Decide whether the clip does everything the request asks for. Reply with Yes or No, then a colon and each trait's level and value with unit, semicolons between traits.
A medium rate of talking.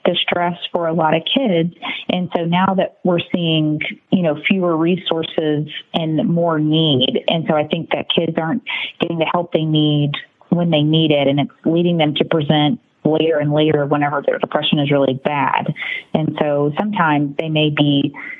Yes: average, 185 wpm